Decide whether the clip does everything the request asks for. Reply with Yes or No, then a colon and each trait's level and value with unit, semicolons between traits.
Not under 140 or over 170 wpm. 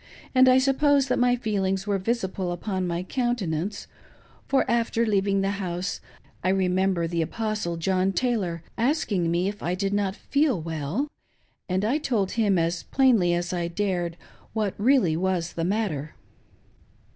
Yes: average, 155 wpm